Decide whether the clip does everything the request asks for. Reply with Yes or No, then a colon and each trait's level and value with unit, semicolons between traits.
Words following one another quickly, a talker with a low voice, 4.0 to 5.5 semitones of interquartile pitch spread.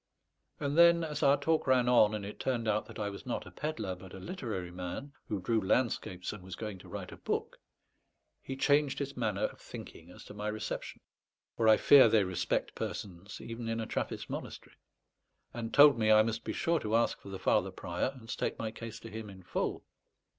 Yes: fast, 215 wpm; low, 110 Hz; average, 4.8 semitones